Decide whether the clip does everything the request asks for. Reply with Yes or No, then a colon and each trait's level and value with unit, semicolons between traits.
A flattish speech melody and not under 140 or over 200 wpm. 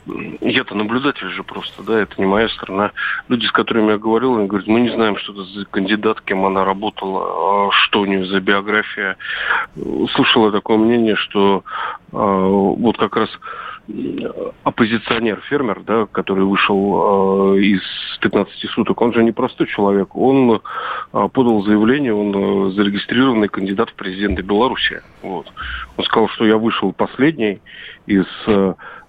Yes: narrow, 2.2 semitones; average, 155 wpm